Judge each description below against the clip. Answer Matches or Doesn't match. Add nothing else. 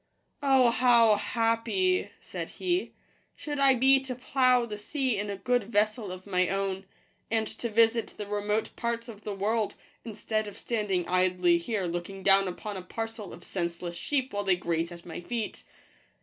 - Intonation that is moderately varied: Matches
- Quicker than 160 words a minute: Matches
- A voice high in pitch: Matches